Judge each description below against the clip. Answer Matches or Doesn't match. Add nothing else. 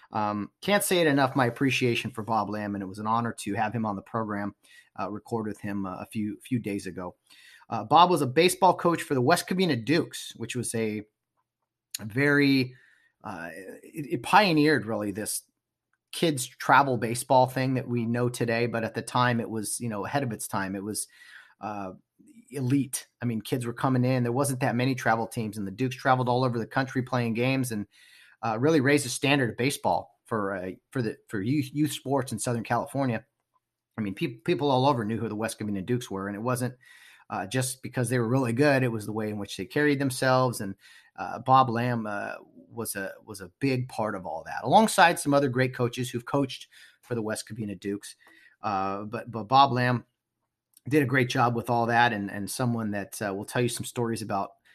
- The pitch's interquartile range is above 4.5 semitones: Doesn't match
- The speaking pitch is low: Matches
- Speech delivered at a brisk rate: Matches